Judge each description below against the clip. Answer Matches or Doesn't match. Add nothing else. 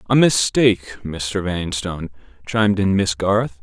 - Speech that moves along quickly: Doesn't match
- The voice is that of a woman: Doesn't match